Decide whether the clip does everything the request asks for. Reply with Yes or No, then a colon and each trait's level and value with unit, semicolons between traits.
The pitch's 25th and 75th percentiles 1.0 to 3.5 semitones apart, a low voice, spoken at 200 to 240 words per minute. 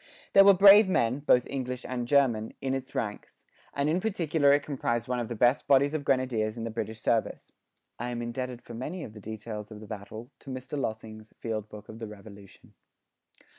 No: average, 4.2 semitones; low, 120 Hz; fast, 205 wpm